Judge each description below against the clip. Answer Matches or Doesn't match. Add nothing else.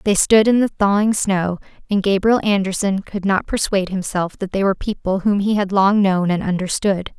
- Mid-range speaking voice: Doesn't match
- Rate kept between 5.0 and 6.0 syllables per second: Matches